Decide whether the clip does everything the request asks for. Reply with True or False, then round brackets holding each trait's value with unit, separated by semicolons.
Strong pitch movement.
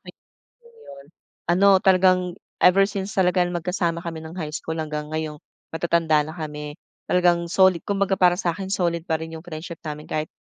False (2.7 semitones)